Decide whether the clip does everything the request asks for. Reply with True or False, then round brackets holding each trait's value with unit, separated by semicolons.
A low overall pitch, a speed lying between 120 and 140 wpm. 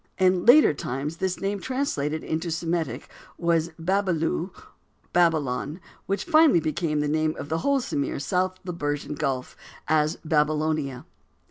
False (160 Hz; 135 wpm)